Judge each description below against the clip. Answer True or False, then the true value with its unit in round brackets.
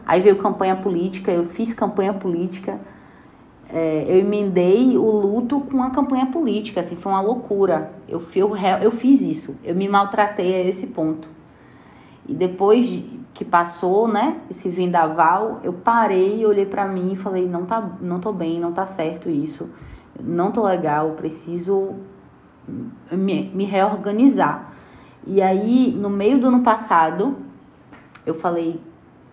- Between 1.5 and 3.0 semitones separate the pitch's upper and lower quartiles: False (3.5 semitones)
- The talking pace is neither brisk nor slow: True (145 wpm)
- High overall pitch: True (195 Hz)